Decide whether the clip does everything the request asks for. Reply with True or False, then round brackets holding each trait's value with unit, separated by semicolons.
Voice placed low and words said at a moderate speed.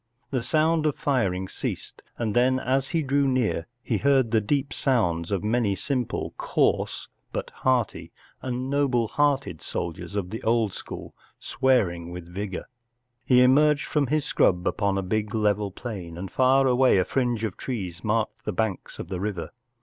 True (115 Hz; 170 wpm)